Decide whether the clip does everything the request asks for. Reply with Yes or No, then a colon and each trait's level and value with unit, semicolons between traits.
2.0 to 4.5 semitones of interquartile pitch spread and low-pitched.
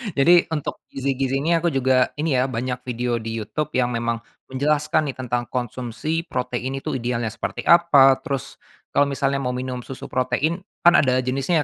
Yes: average, 3.2 semitones; low, 130 Hz